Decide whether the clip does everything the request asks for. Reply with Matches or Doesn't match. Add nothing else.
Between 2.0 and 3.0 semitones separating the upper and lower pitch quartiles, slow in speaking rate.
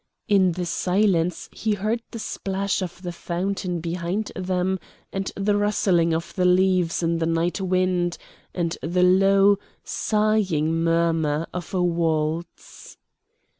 Matches